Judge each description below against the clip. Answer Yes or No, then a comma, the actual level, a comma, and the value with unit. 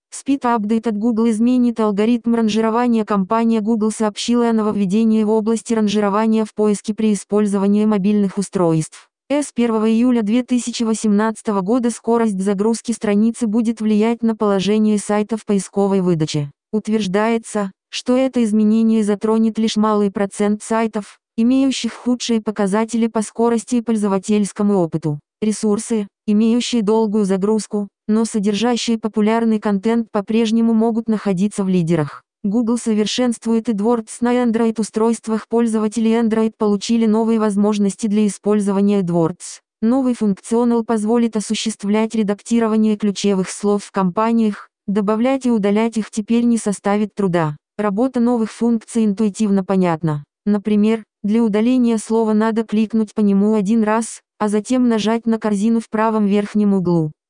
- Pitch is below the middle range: No, high, 220 Hz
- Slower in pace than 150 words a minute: Yes, average, 125 wpm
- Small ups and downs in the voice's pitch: Yes, narrow, 1.8 semitones